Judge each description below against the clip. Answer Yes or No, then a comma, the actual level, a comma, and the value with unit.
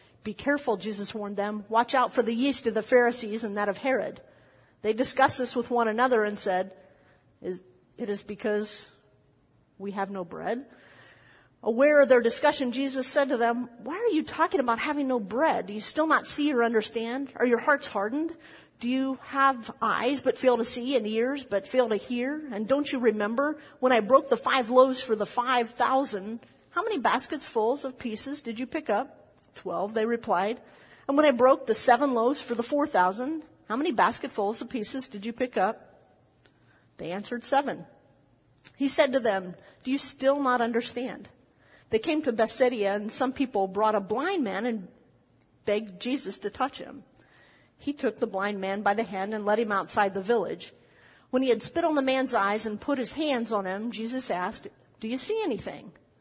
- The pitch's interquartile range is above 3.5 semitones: Yes, average, 4.4 semitones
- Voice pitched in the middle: No, high, 240 Hz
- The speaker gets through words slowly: No, average, 195 wpm